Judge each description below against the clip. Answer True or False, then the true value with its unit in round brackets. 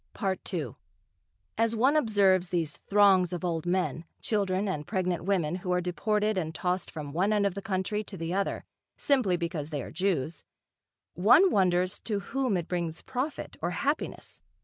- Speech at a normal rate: True (170 wpm)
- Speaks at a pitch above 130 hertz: True (185 Hz)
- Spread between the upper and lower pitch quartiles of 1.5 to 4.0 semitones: True (3.3 semitones)